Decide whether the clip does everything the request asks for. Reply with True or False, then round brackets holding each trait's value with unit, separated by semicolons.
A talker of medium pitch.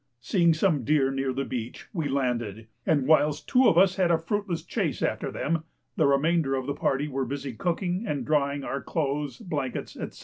True (145 Hz)